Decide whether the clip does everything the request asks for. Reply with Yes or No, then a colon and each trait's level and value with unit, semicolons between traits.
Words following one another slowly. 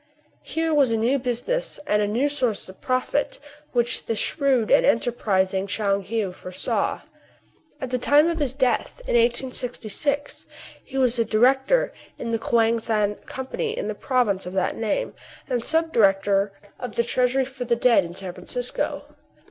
No: average, 165 wpm